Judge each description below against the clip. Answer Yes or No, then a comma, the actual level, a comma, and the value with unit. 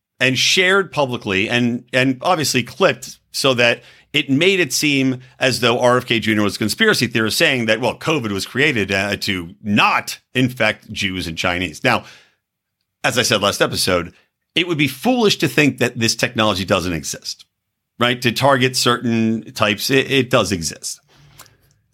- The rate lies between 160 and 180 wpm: Yes, average, 165 wpm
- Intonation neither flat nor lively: Yes, average, 3.9 semitones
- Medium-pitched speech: No, low, 125 Hz